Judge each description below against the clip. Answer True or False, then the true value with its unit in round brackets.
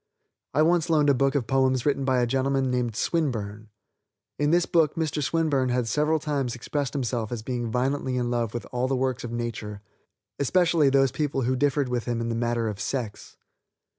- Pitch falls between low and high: False (130 Hz)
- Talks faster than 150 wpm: True (195 wpm)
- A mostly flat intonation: False (3.3 semitones)